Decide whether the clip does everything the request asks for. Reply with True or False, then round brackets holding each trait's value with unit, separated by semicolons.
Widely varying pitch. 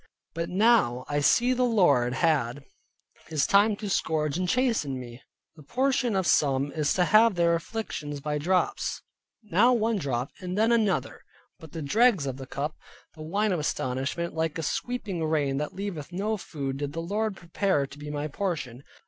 True (6.2 semitones)